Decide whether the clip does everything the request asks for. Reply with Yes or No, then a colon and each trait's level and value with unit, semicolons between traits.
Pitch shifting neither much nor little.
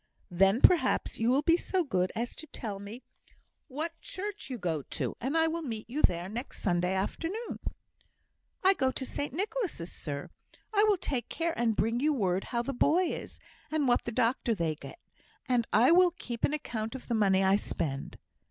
No: wide, 8.1 semitones